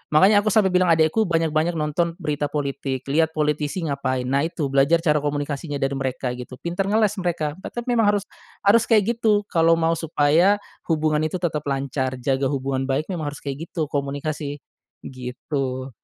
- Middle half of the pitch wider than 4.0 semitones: No, average, 3.7 semitones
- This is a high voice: No, medium, 150 Hz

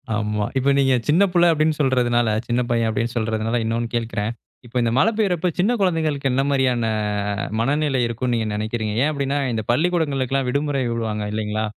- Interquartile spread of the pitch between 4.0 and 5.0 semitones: Yes, average, 4.5 semitones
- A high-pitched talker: No, low, 125 Hz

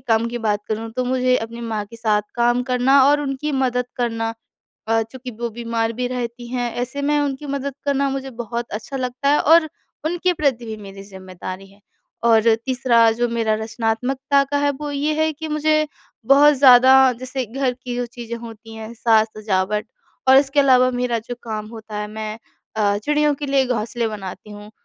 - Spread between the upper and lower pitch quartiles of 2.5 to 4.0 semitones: Yes, average, 3.4 semitones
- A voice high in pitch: Yes, high, 245 Hz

